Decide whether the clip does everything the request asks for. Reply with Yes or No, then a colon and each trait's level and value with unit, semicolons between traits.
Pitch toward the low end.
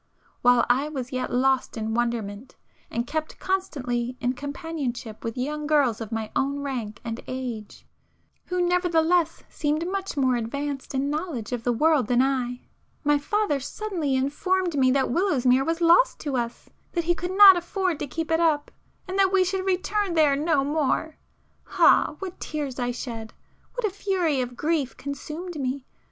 No: very high, 285 Hz